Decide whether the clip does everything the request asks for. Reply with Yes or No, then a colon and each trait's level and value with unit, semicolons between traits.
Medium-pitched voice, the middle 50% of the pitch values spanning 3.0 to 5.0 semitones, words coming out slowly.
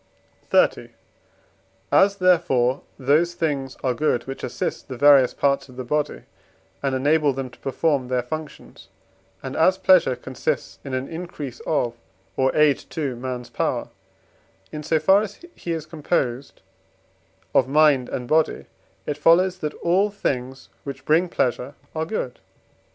No: medium, 145 Hz; average, 3.8 semitones; average, 150 wpm